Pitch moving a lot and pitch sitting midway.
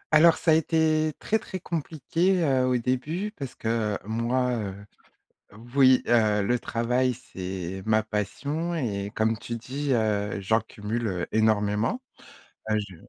No: wide, 5.7 semitones; low, 120 Hz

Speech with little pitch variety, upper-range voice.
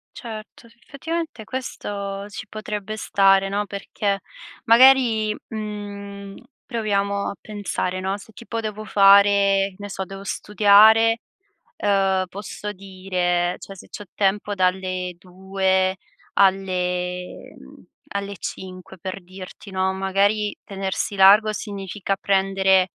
Yes: narrow, 1.6 semitones; high, 200 Hz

